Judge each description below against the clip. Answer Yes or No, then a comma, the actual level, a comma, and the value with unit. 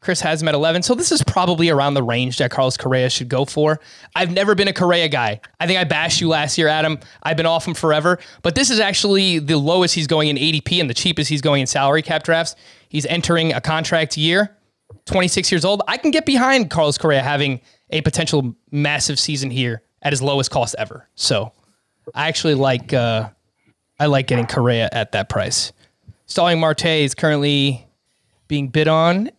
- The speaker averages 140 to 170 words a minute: No, fast, 205 wpm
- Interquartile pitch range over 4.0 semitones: No, average, 3.5 semitones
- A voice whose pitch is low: No, medium, 155 Hz